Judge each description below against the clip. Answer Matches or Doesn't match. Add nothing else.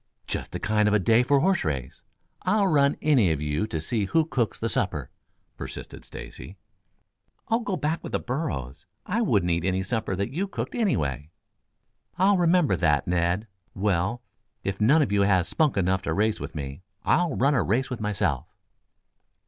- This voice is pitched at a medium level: Doesn't match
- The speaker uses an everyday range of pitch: Doesn't match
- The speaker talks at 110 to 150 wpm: Doesn't match